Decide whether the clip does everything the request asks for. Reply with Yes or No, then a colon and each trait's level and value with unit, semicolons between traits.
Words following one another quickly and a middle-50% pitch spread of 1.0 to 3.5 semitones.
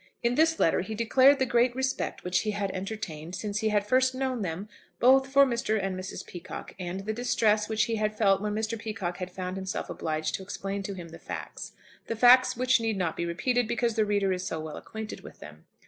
No: fast, 225 wpm; average, 4.2 semitones